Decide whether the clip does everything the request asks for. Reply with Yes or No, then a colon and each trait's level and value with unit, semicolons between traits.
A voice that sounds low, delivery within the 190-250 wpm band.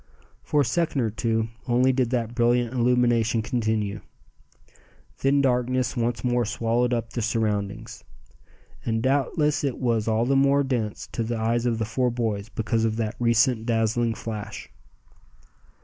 No: low, 120 Hz; average, 150 wpm